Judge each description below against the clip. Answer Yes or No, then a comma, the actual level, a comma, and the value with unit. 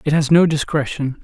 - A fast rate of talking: No, average, 195 wpm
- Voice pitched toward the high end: No, medium, 150 Hz